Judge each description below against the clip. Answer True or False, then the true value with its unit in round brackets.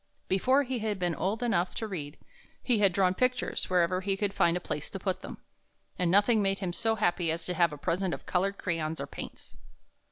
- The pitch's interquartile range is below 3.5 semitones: True (3.1 semitones)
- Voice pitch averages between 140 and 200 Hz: True (190 Hz)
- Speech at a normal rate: False (220 wpm)